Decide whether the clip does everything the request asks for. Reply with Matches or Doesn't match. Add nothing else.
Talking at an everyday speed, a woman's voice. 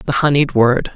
Matches